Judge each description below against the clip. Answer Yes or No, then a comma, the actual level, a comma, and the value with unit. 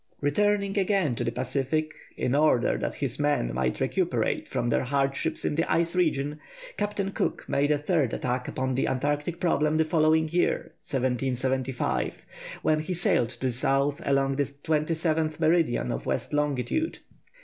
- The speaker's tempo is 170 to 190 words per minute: No, average, 160 wpm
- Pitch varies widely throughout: No, average, 3.4 semitones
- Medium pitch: Yes, medium, 145 Hz